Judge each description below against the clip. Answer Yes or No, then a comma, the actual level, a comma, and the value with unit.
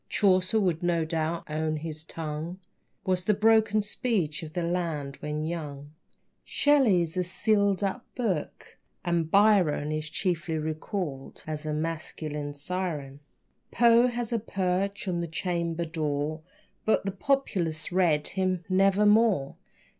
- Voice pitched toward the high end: No, medium, 175 Hz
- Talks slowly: Yes, slow, 130 wpm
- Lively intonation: No, average, 4.2 semitones